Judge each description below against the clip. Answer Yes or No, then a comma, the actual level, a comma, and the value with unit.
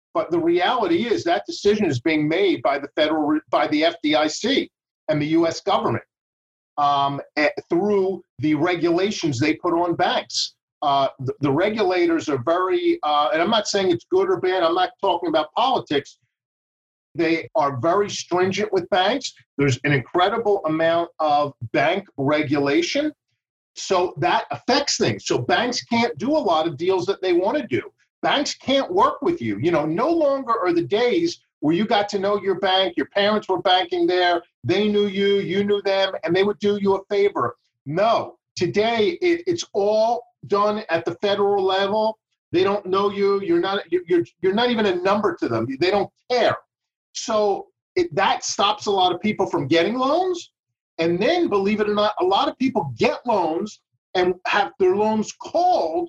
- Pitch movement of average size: No, wide, 7.5 semitones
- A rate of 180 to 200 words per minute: Yes, average, 185 wpm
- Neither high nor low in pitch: No, high, 200 Hz